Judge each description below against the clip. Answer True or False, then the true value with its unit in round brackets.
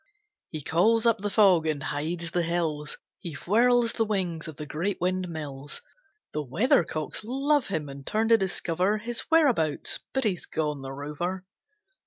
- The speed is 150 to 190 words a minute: True (160 wpm)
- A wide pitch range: True (5.9 semitones)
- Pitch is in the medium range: True (175 Hz)